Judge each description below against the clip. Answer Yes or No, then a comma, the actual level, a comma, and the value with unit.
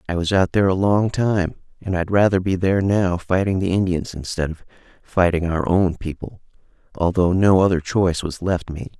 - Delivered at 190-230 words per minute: Yes, average, 195 wpm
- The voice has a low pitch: Yes, very low, 90 Hz